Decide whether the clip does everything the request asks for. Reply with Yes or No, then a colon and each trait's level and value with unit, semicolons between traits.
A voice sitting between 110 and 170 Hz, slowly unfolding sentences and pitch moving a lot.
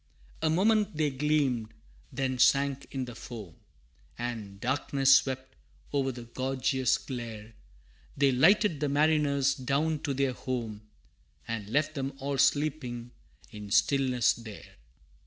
No: low, 135 Hz; slow, 125 wpm; average, 3.1 semitones